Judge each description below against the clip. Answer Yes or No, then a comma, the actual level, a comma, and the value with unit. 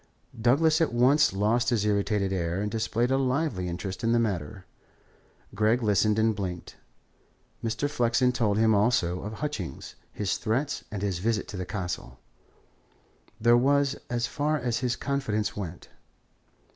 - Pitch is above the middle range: No, low, 110 Hz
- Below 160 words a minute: Yes, average, 150 wpm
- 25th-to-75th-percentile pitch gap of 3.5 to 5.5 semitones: Yes, average, 3.9 semitones